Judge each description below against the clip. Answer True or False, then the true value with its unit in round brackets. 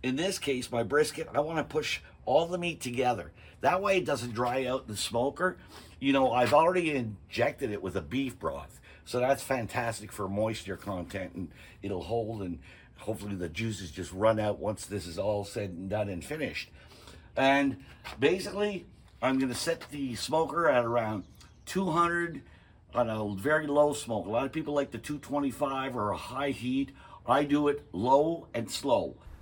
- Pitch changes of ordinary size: False (6.3 semitones)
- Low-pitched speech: True (125 Hz)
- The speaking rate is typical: True (180 wpm)